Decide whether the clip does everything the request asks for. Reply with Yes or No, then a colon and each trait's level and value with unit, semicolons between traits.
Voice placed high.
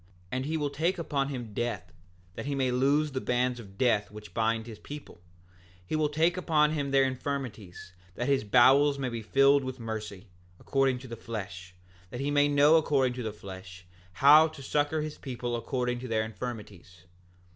No: low, 125 Hz